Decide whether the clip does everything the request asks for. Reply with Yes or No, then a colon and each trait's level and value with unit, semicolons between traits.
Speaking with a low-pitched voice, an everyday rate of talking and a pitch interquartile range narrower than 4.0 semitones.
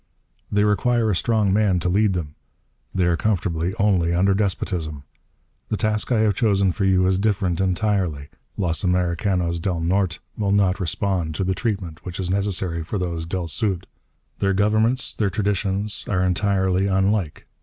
Yes: very low, 95 Hz; average, 165 wpm; average, 2.7 semitones